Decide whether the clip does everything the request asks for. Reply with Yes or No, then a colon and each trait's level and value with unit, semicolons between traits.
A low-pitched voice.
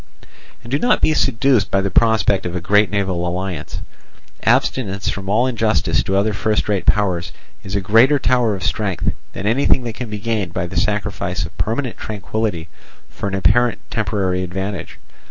Yes: low, 105 Hz